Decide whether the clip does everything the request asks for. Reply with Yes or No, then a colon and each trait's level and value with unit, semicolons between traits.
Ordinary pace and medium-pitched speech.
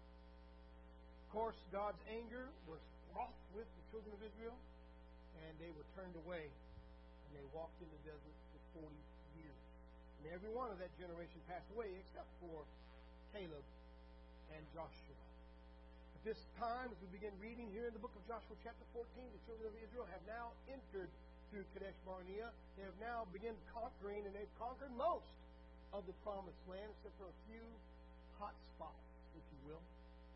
Yes: average, 170 wpm; medium, 175 Hz